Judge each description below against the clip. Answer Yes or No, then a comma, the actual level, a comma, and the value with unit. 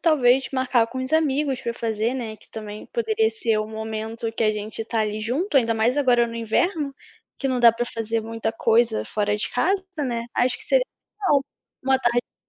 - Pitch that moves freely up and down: No, average, 3.3 semitones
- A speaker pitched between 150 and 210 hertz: No, high, 240 Hz